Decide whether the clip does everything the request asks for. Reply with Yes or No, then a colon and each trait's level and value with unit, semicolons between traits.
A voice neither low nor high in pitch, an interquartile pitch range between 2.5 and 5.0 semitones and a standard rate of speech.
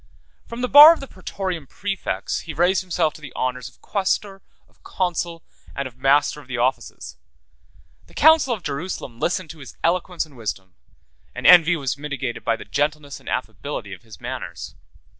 No: medium, 160 Hz; wide, 5.6 semitones; average, 180 wpm